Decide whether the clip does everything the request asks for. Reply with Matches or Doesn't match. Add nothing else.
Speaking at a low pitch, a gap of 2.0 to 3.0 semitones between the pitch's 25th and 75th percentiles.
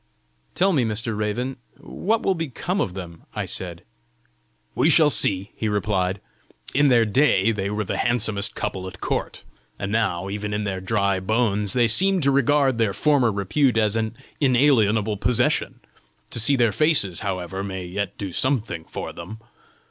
Doesn't match